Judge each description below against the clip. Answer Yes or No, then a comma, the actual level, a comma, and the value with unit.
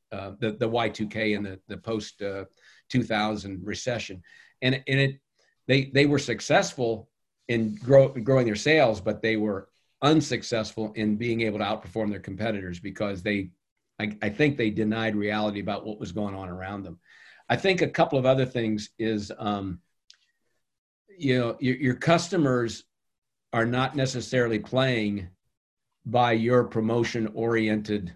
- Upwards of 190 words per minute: No, average, 160 wpm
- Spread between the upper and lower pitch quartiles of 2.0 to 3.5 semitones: Yes, average, 3.2 semitones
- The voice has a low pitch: Yes, low, 110 Hz